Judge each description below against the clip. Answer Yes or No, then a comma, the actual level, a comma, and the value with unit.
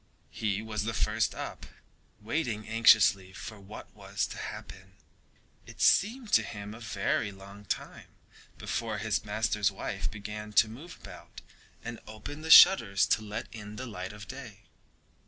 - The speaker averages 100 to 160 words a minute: Yes, average, 155 wpm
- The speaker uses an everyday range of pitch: No, narrow, 1.8 semitones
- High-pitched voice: No, low, 105 Hz